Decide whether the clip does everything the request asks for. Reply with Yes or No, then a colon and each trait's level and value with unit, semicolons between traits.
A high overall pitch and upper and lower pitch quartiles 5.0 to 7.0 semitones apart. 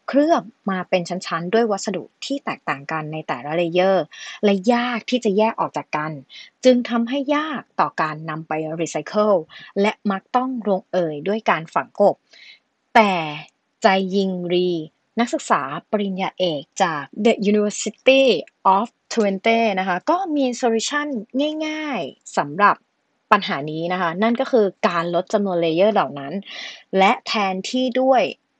Yes: high, 205 Hz; wide, 5.6 semitones